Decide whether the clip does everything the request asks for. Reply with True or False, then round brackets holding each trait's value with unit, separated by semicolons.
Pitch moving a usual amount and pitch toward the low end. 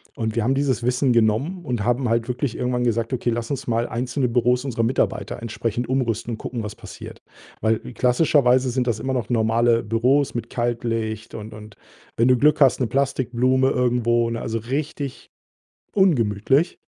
False (2.2 semitones; 120 Hz)